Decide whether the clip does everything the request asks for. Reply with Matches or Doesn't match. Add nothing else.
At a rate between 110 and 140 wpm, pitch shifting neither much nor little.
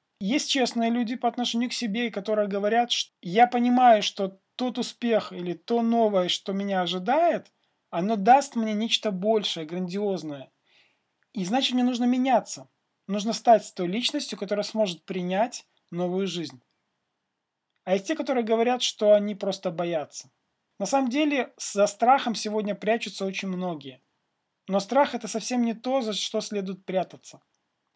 Doesn't match